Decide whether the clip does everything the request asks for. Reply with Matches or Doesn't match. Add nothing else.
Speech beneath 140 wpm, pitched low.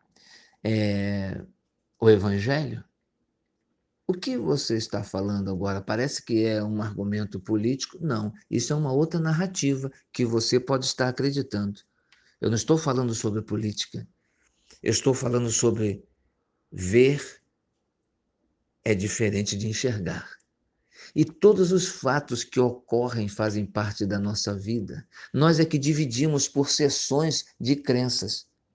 Matches